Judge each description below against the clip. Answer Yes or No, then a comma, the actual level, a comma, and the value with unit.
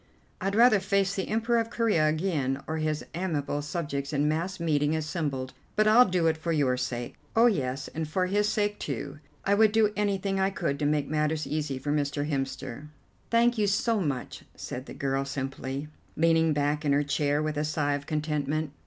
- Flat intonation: No, average, 5.2 semitones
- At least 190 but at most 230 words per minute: Yes, average, 195 wpm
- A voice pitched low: No, medium, 155 Hz